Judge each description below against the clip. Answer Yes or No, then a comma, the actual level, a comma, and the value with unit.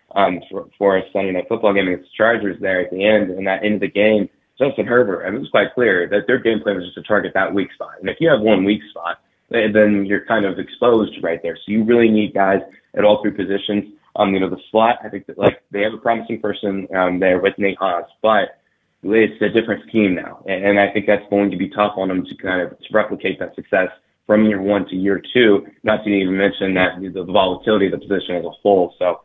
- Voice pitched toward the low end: Yes, low, 100 Hz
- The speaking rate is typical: No, fast, 250 wpm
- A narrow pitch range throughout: Yes, narrow, 1.9 semitones